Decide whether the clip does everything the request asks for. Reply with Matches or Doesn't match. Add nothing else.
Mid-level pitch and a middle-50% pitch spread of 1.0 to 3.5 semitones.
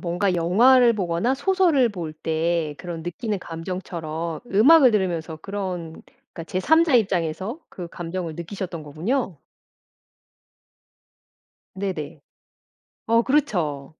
Doesn't match